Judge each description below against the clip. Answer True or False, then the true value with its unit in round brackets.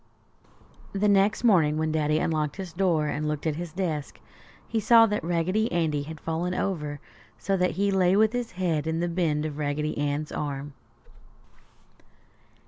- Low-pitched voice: False (165 Hz)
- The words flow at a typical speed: True (165 wpm)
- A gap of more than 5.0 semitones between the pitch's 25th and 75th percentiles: False (4.1 semitones)